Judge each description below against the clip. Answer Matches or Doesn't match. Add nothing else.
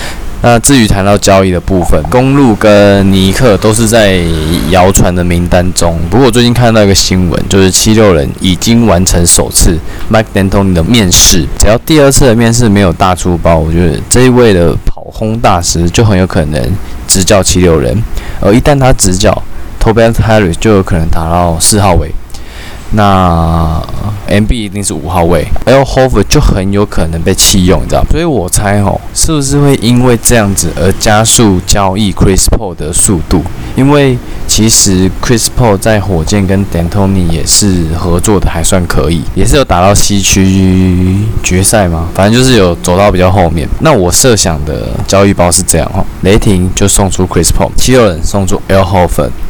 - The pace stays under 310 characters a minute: Doesn't match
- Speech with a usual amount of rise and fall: Matches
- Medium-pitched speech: Doesn't match